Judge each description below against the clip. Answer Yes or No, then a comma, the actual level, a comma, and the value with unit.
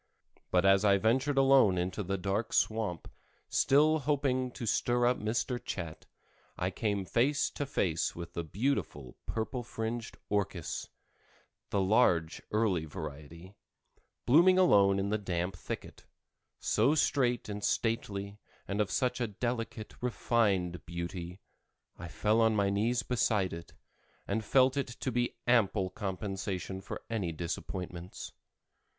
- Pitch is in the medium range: No, low, 105 Hz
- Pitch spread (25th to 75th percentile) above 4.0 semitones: Yes, average, 4.8 semitones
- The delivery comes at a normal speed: No, slow, 130 wpm